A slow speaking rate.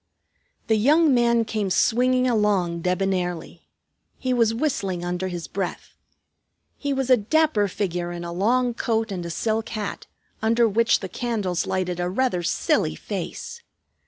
No: average, 150 wpm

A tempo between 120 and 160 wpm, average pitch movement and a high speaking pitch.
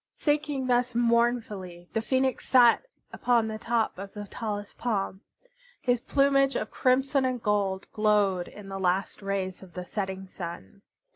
Yes: average, 150 wpm; average, 4.3 semitones; high, 215 Hz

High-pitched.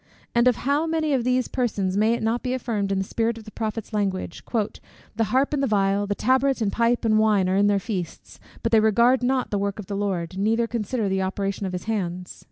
Yes: high, 215 Hz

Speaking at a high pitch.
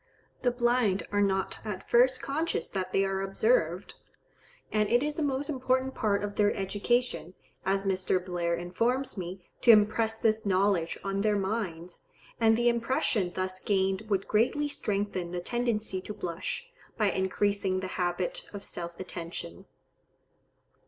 Yes: high, 205 Hz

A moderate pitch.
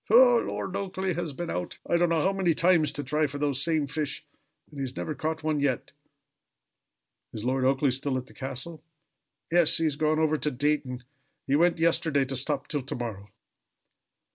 Yes: medium, 150 Hz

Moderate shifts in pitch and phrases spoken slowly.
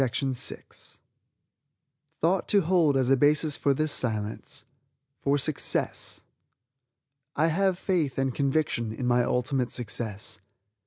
Yes: average, 4.2 semitones; slow, 110 wpm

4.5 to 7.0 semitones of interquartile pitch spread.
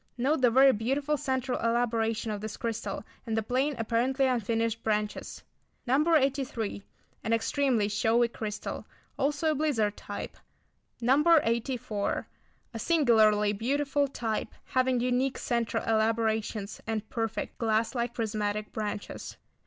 No: average, 3.3 semitones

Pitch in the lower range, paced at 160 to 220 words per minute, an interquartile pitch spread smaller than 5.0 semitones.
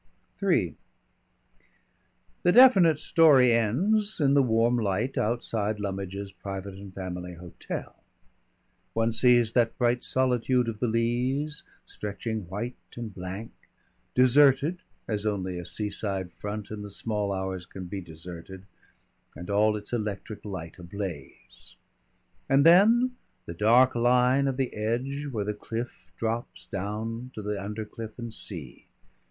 No: low, 110 Hz; slow, 135 wpm; average, 4.2 semitones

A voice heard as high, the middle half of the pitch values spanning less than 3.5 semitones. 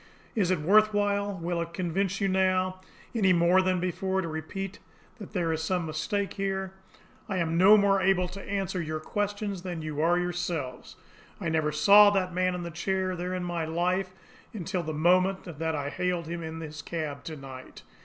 No: medium, 180 Hz; average, 2.9 semitones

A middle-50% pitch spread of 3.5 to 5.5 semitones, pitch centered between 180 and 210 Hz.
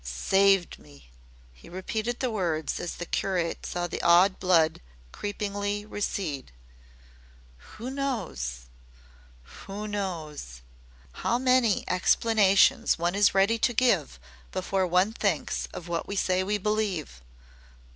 Yes: average, 4.0 semitones; high, 190 Hz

